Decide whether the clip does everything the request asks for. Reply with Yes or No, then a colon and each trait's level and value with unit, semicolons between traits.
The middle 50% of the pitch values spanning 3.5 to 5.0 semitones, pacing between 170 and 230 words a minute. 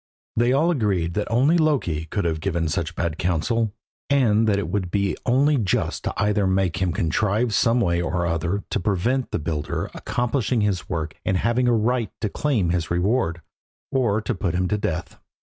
No: wide, 5.4 semitones; average, 190 wpm